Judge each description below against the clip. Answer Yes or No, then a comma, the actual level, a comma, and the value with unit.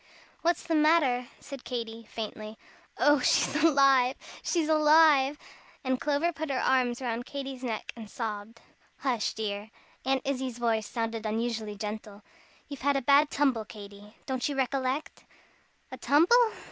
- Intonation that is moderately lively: Yes, average, 4.1 semitones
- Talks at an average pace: Yes, average, 145 wpm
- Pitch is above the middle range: Yes, very high, 255 Hz